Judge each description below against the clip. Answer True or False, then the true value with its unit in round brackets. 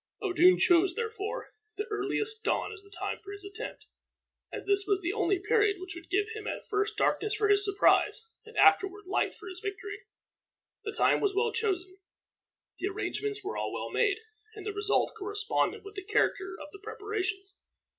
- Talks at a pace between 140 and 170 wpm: False (185 wpm)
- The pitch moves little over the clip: True (1.6 semitones)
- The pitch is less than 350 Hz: False (405 Hz)